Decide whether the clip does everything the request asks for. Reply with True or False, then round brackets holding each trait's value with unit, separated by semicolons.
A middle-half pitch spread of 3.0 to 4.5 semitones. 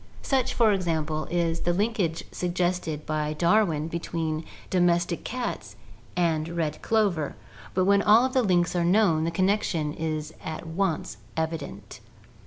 True (3.3 semitones)